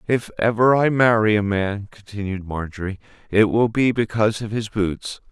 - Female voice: No, male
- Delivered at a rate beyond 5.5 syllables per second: No, 4.9 syllables/s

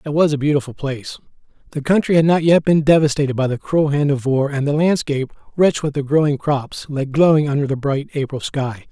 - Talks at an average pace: No, fast, 220 wpm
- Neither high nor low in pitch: Yes, medium, 145 Hz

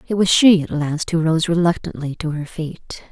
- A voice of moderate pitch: Yes, medium, 165 Hz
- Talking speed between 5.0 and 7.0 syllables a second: No, 4.8 syllables/s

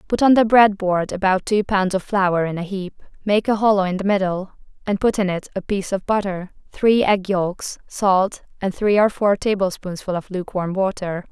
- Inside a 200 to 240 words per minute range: Yes, fast, 205 wpm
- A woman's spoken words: Yes, female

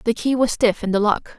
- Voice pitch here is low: No, high, 225 Hz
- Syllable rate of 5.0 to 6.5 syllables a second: Yes, 5.5 syllables/s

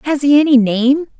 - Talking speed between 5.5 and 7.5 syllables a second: No, 5.2 syllables/s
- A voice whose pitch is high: Yes, very high, 275 Hz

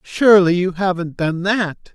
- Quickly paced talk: No, average, 155 wpm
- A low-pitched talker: No, medium, 185 Hz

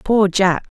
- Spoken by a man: No, female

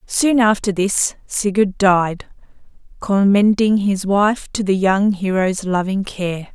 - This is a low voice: No, high, 200 Hz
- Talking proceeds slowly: Yes, slow, 130 wpm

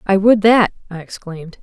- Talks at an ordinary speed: Yes, average, 185 wpm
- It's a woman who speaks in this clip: Yes, female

